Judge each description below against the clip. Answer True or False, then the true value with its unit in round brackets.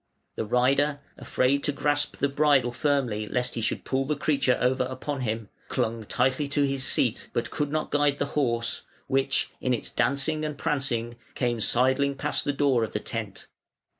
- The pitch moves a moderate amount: True (3.1 semitones)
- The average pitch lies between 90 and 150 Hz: True (135 Hz)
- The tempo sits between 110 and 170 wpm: False (180 wpm)